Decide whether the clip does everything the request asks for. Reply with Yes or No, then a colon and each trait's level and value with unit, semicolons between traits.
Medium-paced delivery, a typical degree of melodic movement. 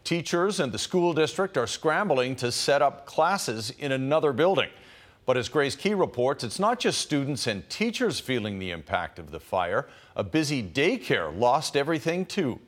No: average, 175 wpm; wide, 6.0 semitones